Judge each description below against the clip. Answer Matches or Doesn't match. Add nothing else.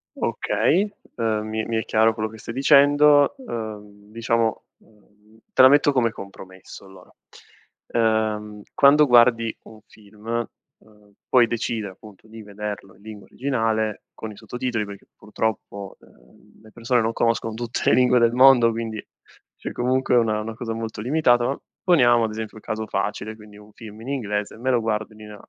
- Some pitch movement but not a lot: Doesn't match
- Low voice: Matches